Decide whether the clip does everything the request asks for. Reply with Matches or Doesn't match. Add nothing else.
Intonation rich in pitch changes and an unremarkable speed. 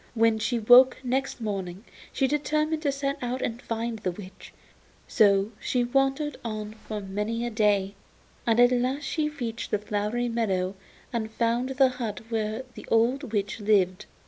Doesn't match